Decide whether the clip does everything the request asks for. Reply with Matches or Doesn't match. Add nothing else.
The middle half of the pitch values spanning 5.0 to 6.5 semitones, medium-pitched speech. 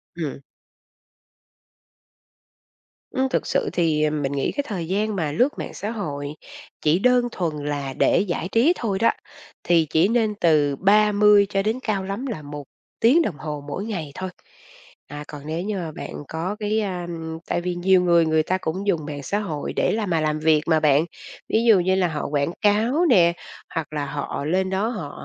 Matches